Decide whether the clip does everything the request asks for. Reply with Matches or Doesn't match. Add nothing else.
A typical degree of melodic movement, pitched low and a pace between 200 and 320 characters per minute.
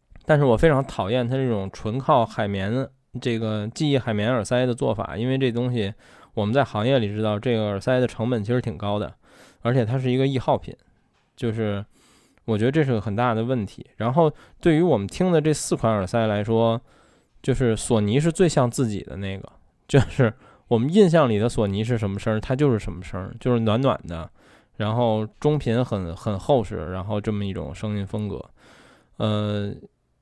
Matches